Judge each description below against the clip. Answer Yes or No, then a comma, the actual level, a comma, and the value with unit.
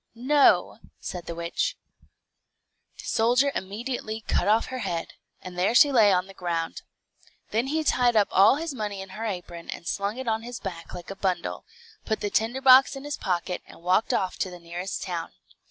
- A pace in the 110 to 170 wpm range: No, average, 190 wpm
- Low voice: No, high, 205 Hz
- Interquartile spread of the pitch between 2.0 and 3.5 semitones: No, average, 5.2 semitones